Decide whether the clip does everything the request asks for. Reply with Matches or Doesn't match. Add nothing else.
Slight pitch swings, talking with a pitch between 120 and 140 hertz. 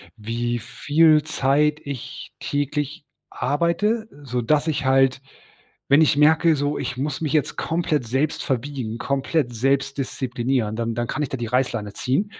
Doesn't match